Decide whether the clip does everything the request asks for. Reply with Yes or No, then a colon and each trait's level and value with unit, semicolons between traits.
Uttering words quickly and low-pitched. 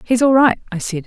No: fast, 285 wpm; high, 230 Hz